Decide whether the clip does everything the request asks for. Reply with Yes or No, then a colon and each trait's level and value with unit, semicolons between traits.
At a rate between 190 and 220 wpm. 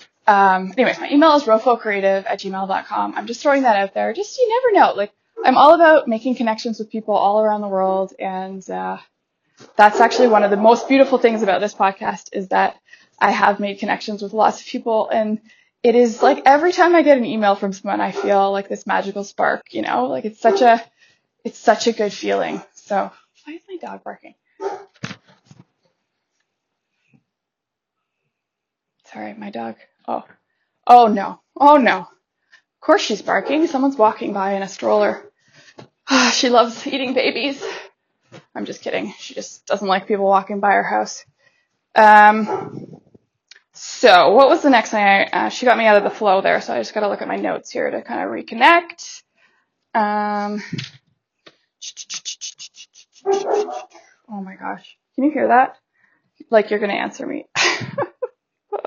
No: average, 170 wpm